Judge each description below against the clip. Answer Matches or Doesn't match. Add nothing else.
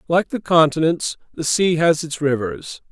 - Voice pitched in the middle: Matches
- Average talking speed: Matches